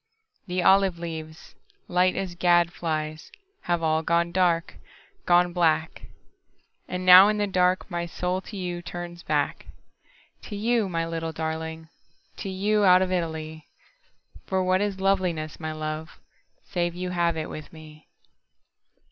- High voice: No, medium, 175 Hz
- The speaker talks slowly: Yes, slow, 120 wpm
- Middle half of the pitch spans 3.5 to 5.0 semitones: No, narrow, 2.4 semitones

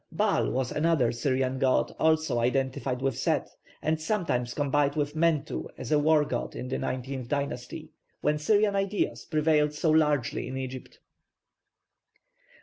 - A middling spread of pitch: Yes, average, 3.2 semitones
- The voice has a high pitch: No, medium, 145 Hz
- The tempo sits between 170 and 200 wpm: No, average, 145 wpm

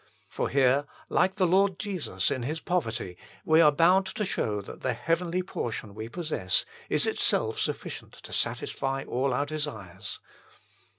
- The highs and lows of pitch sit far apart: Yes, wide, 6.6 semitones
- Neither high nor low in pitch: Yes, medium, 150 Hz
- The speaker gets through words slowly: No, average, 155 wpm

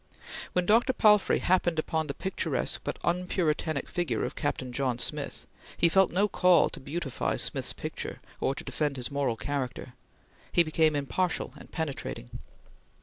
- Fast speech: No, average, 150 wpm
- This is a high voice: No, medium, 160 Hz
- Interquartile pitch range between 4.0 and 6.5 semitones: Yes, average, 4.5 semitones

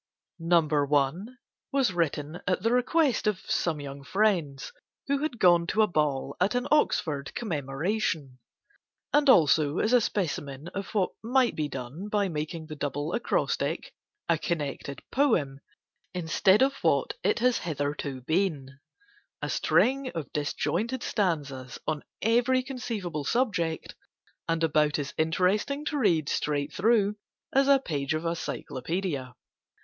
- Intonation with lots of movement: Yes, wide, 7.6 semitones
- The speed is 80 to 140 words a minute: Yes, slow, 135 wpm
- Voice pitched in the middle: Yes, medium, 170 Hz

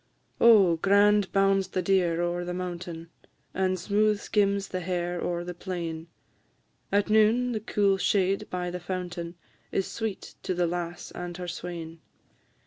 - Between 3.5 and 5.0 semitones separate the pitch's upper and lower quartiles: No, narrow, 2.4 semitones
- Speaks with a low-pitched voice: No, medium, 180 Hz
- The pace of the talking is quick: No, average, 155 wpm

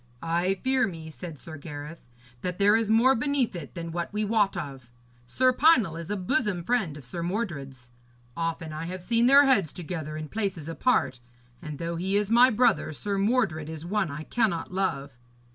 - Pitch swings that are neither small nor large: No, wide, 5.8 semitones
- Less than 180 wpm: No, average, 190 wpm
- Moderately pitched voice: Yes, medium, 180 Hz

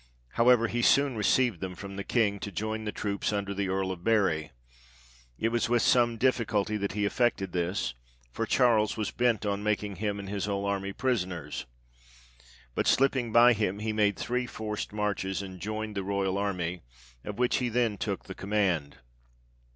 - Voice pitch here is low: Yes, low, 105 Hz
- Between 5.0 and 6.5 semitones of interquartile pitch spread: No, average, 2.9 semitones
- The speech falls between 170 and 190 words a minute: Yes, average, 180 wpm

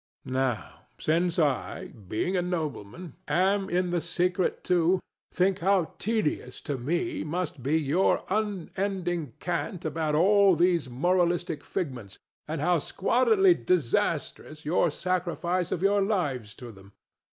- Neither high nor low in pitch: Yes, medium, 175 Hz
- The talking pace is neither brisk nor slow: No, slow, 130 wpm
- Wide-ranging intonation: No, average, 3.8 semitones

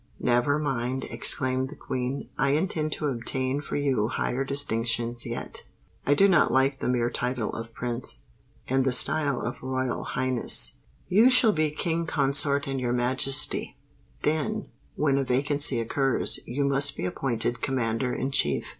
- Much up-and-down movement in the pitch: No, average, 2.7 semitones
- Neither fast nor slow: Yes, average, 155 wpm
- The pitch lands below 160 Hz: Yes, low, 135 Hz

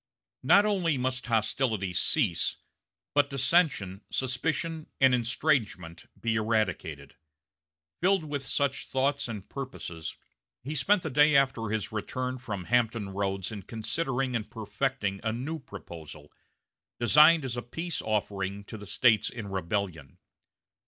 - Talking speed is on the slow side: Yes, slow, 130 wpm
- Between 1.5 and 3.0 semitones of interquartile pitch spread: No, average, 5.3 semitones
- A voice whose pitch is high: No, low, 120 Hz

